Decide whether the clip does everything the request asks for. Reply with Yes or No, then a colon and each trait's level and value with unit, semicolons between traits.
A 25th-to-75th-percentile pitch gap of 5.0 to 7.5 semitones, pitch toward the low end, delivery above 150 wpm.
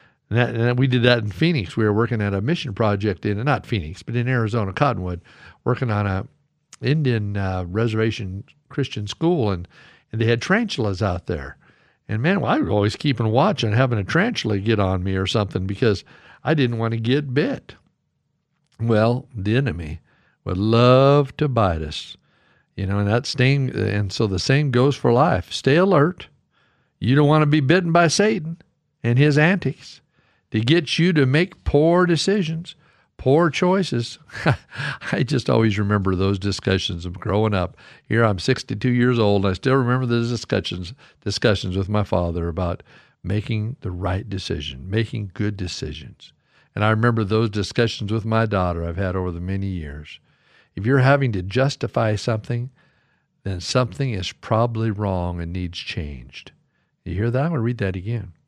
Yes: average, 5.3 semitones; low, 115 Hz; average, 175 wpm